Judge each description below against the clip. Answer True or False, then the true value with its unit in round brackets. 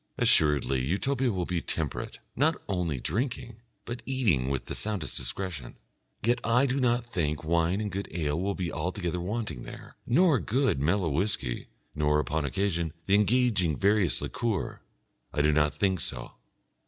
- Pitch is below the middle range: True (95 Hz)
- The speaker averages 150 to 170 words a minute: True (155 wpm)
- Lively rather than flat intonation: True (7.1 semitones)